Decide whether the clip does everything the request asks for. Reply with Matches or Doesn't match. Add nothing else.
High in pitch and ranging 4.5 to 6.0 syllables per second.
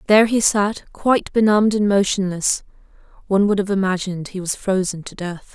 Matches